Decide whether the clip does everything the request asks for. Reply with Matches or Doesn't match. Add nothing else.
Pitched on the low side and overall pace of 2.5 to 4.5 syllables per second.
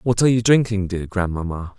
Doesn't match